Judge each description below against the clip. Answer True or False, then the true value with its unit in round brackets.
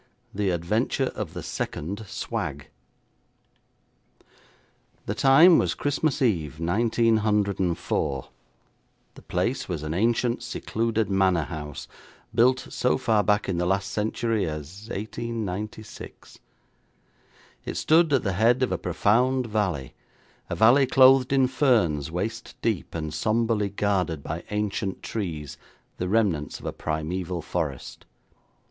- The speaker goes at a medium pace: False (120 wpm)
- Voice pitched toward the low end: True (105 Hz)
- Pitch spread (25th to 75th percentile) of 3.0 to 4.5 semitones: False (5.1 semitones)